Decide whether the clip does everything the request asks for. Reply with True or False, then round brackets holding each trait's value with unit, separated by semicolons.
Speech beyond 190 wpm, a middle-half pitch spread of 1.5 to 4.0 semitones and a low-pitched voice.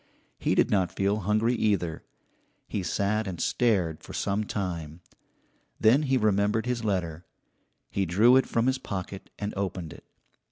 False (155 wpm; 3.3 semitones; 100 Hz)